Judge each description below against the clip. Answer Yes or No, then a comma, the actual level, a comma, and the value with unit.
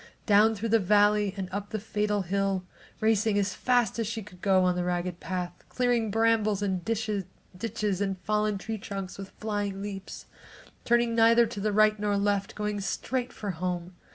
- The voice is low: No, high, 205 Hz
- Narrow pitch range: Yes, narrow, 2.2 semitones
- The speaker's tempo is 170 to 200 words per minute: Yes, average, 180 wpm